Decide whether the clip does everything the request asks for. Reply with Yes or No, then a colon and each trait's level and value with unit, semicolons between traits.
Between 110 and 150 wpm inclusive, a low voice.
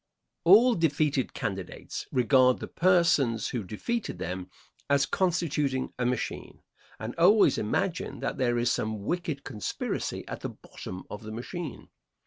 Yes: slow, 135 wpm; low, 130 Hz